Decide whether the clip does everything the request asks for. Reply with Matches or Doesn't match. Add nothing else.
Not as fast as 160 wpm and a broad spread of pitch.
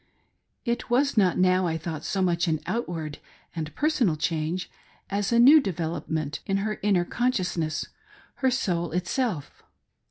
Matches